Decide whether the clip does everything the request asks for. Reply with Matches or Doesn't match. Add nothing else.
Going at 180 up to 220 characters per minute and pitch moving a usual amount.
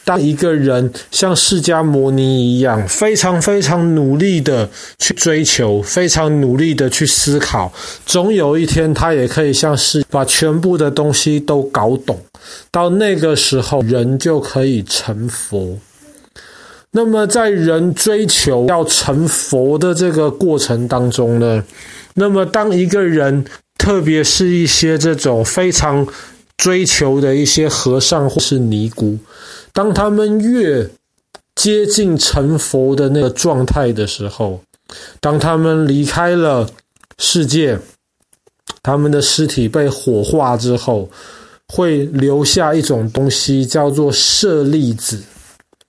Matches